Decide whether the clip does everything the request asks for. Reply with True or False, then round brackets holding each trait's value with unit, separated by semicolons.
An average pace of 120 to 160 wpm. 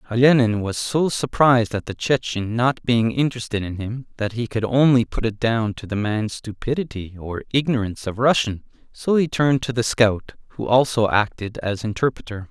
False (180 wpm)